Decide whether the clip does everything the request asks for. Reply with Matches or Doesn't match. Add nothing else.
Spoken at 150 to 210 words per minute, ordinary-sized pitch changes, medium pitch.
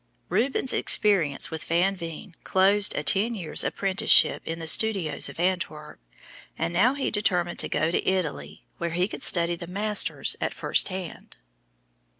Matches